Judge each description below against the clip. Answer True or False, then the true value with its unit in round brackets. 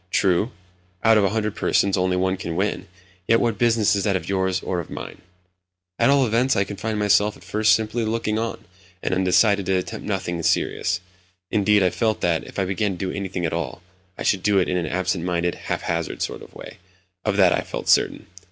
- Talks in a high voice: False (95 Hz)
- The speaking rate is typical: False (215 wpm)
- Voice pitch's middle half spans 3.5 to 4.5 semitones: False (2.7 semitones)